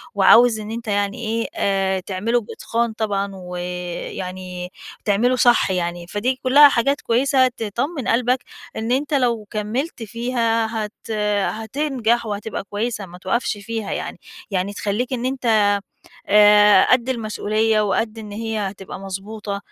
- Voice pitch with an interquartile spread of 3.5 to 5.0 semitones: No, average, 3.1 semitones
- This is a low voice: No, high, 220 Hz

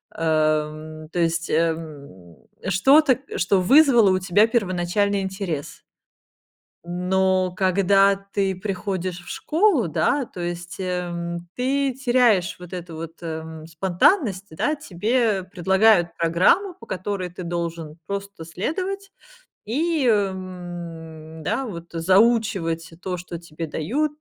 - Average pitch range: Yes, average, 3.9 semitones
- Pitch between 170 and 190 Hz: Yes, medium, 185 Hz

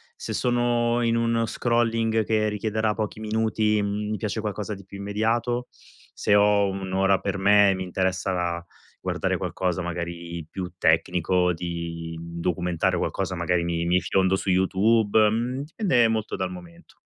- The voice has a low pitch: Yes, low, 100 Hz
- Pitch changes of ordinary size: Yes, average, 3.6 semitones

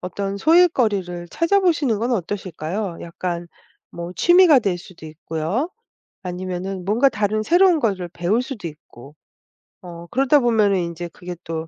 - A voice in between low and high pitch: No, high, 195 Hz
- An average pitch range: No, wide, 6.0 semitones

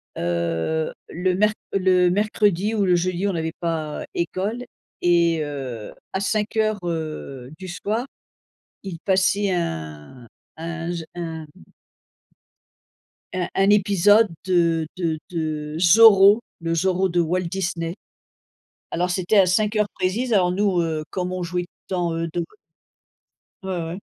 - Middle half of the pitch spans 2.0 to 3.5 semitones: Yes, average, 2.9 semitones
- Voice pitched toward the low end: No, medium, 180 Hz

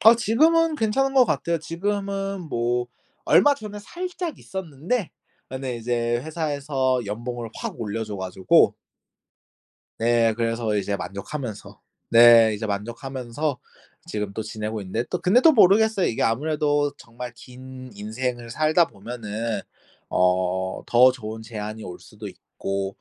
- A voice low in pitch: Yes, low, 125 Hz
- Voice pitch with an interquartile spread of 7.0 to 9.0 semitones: Yes, wide, 7.3 semitones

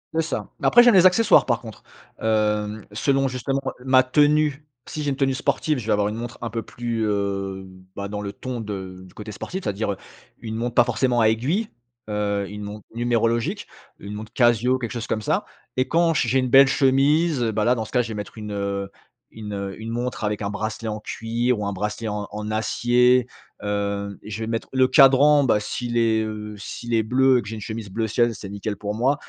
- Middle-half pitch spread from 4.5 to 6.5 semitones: No, average, 3.6 semitones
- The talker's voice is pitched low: Yes, low, 115 Hz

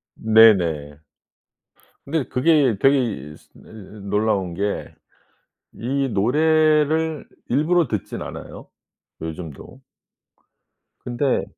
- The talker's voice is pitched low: Yes, low, 125 Hz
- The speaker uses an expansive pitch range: Yes, wide, 7.2 semitones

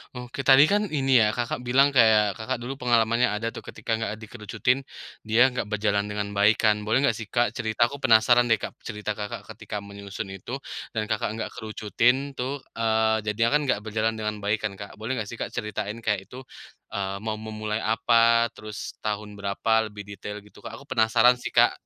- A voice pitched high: No, low, 110 Hz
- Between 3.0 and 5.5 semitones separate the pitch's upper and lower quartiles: No, narrow, 2.4 semitones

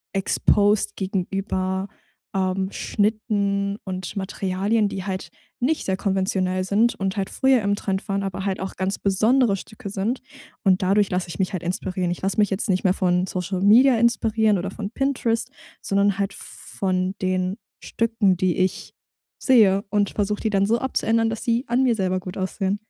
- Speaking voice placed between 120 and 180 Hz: No, high, 195 Hz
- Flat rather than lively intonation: Yes, narrow, 2.3 semitones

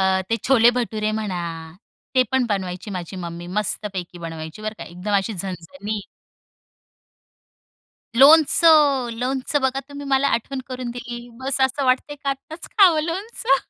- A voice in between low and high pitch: No, high, 245 Hz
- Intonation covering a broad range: Yes, wide, 5.7 semitones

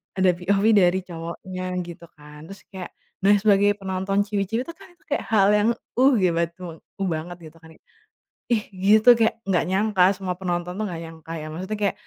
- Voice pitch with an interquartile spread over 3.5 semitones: No, average, 3.0 semitones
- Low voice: No, high, 190 Hz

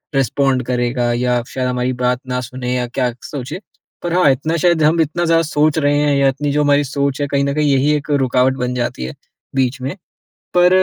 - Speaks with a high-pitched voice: No, medium, 140 Hz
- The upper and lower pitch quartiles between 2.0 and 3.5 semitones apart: Yes, average, 2.9 semitones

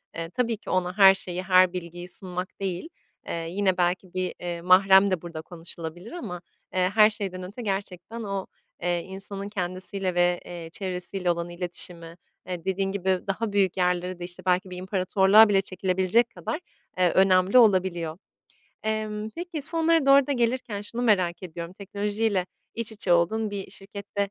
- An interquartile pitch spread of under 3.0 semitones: Yes, narrow, 2.5 semitones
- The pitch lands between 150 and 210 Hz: Yes, high, 190 Hz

